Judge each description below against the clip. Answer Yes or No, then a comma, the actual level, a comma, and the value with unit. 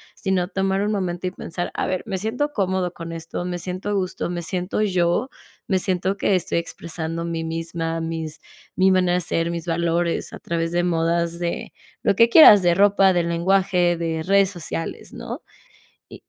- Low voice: No, medium, 175 Hz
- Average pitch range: No, narrow, 2.3 semitones